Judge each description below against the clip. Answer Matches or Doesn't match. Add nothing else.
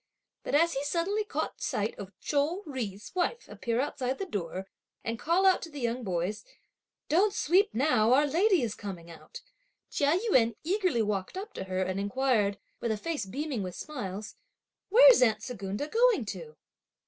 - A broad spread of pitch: Matches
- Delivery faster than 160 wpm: Matches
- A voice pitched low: Doesn't match